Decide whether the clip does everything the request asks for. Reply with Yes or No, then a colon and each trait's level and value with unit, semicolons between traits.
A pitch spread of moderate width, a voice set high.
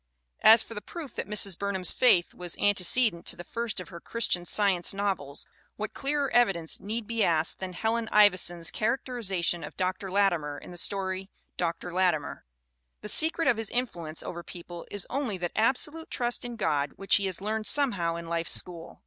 Yes: average, 4.7 semitones; high, 195 Hz